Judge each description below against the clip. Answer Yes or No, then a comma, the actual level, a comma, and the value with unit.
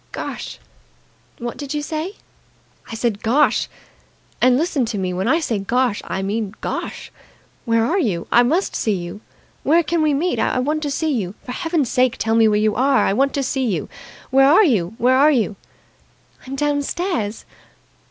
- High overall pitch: Yes, very high, 255 Hz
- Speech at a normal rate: Yes, average, 185 wpm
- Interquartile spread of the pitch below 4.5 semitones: No, average, 5.3 semitones